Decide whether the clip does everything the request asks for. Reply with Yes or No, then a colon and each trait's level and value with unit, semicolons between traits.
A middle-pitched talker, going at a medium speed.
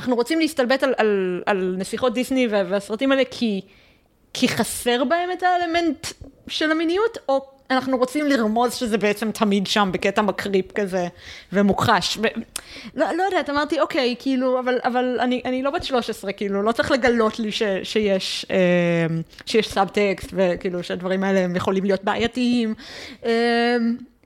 No: high, 230 Hz; average, 140 wpm